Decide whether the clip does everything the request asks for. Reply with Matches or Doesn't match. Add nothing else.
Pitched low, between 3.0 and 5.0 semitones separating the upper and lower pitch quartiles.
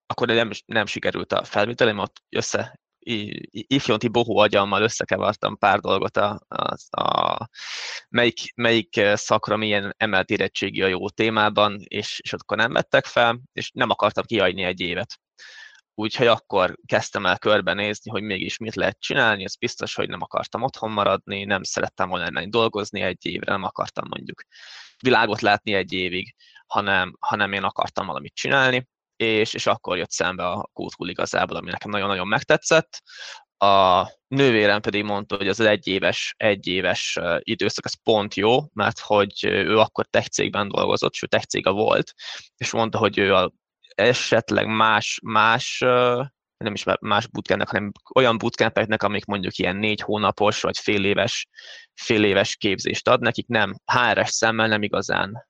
Doesn't match